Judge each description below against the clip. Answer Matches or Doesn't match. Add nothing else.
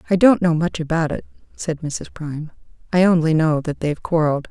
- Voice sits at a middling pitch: Matches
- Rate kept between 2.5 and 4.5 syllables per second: Doesn't match